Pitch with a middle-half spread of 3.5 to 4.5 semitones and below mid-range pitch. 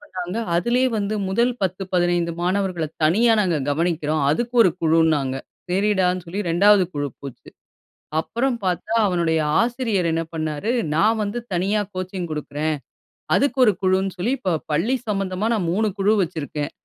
No: average, 4.2 semitones; medium, 185 Hz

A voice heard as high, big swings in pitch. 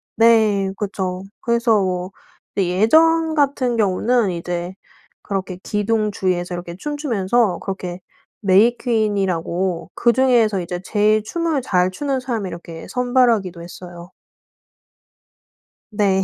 No: high, 205 Hz; average, 4.5 semitones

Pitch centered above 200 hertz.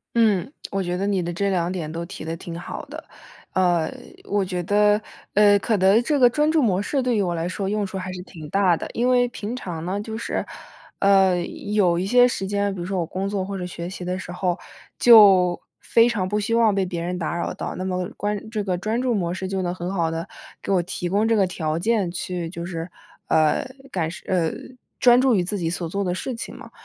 No: high, 190 Hz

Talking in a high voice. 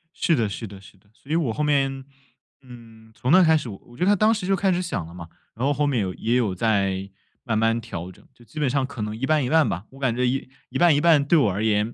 No: low, 125 Hz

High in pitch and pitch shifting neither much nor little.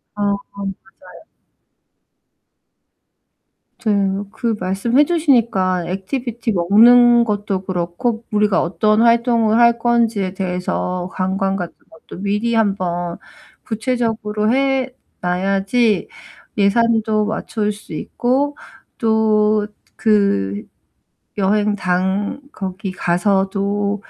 Yes: high, 210 Hz; average, 3.3 semitones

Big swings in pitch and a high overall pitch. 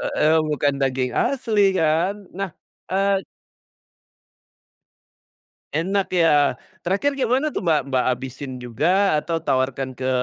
No: wide, 6.6 semitones; medium, 160 Hz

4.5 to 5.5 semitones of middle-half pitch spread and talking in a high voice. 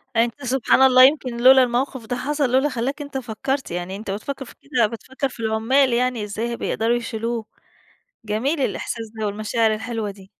No: average, 3.2 semitones; high, 240 Hz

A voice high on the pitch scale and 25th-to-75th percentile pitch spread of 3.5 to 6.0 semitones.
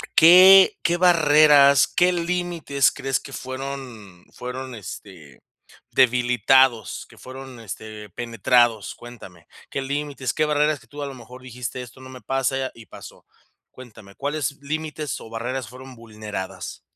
No: low, 130 Hz; average, 3.8 semitones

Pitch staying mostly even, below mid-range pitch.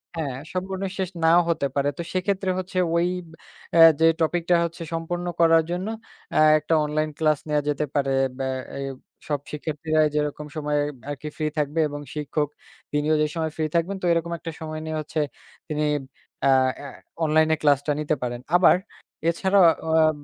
No: narrow, 2.2 semitones; medium, 155 Hz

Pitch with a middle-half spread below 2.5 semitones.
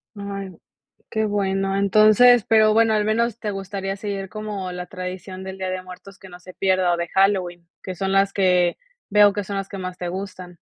Yes: narrow, 1.9 semitones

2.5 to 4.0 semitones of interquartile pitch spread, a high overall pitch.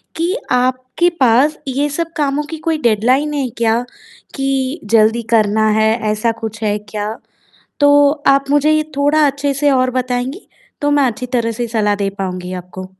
No: average, 4.8 semitones; very high, 255 Hz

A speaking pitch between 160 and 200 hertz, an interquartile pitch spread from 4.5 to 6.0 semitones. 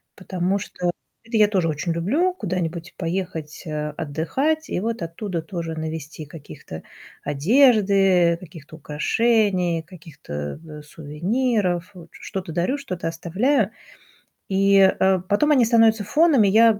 Yes: medium, 185 Hz; average, 5.1 semitones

